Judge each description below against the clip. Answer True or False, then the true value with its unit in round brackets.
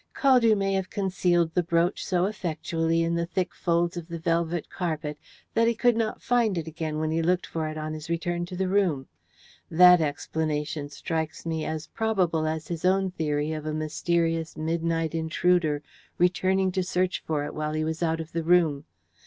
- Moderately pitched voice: True (165 Hz)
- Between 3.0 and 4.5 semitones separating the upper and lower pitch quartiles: False (2.4 semitones)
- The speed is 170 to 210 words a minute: True (190 wpm)